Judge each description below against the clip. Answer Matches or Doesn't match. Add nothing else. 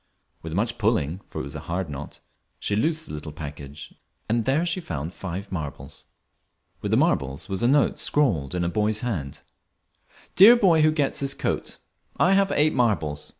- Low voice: Matches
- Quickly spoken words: Doesn't match